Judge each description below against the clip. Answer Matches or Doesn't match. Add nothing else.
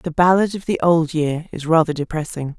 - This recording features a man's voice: Doesn't match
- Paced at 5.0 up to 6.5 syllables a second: Matches